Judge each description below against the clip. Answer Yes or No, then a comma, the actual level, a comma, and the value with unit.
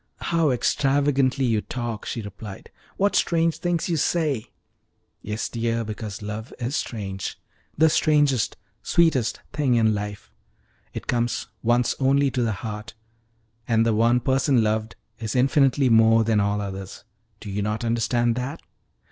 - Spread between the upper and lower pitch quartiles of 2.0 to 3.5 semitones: No, average, 4.0 semitones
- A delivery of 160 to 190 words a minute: No, average, 145 wpm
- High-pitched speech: No, low, 120 Hz